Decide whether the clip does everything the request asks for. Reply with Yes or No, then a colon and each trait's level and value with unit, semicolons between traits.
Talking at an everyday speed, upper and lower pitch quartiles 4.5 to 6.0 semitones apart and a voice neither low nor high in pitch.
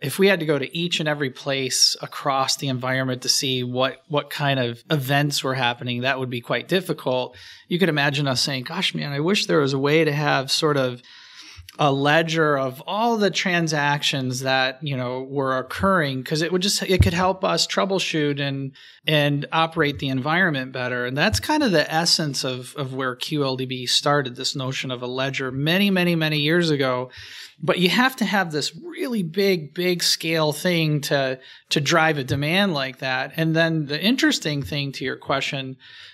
No: average, 195 wpm; average, 4.0 semitones; medium, 145 Hz